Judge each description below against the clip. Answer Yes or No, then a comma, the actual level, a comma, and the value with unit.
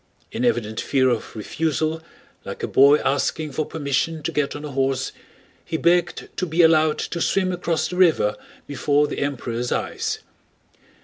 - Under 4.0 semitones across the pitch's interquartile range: Yes, average, 3.4 semitones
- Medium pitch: Yes, medium, 150 Hz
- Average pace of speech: Yes, average, 165 wpm